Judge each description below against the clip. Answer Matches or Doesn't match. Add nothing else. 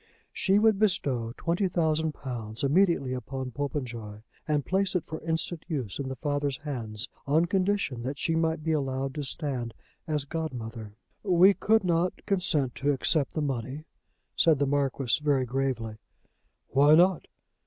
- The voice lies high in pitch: Doesn't match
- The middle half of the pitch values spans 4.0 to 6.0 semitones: Matches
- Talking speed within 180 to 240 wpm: Doesn't match